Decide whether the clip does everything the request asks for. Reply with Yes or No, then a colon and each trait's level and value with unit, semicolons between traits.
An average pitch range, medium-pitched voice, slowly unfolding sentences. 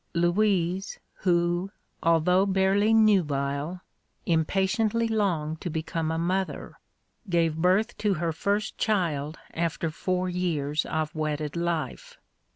Yes: average, 3.4 semitones; medium, 175 Hz; slow, 110 wpm